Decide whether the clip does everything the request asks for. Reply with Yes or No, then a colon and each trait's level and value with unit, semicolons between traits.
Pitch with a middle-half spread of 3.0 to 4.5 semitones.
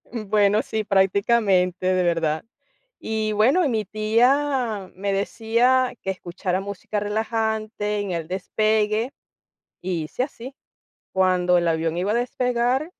Yes: average, 3.7 semitones